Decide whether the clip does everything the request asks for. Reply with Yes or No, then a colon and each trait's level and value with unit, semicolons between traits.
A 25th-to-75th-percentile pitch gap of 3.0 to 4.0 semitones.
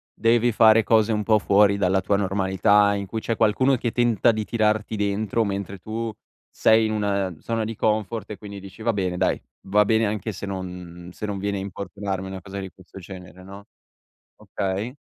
No: narrow, 2.4 semitones